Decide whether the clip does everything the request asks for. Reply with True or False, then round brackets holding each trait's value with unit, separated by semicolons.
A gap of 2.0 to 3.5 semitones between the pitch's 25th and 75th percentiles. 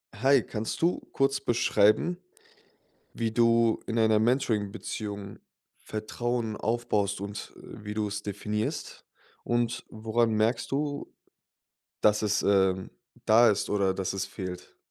True (2.7 semitones)